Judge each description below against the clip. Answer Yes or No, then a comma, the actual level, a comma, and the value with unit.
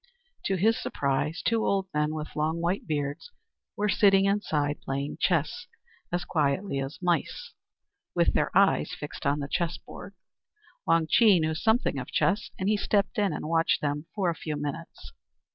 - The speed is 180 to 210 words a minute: No, average, 165 wpm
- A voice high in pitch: No, medium, 165 Hz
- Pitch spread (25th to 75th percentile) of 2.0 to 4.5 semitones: No, average, 5.0 semitones